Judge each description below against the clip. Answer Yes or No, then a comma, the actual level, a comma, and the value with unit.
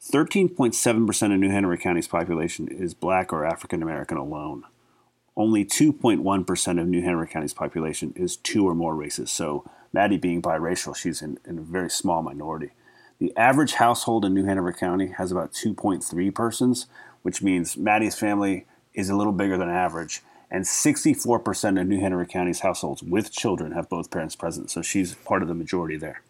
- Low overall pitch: Yes, very low, 95 Hz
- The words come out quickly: No, average, 175 wpm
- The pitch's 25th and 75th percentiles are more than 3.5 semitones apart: No, narrow, 2.6 semitones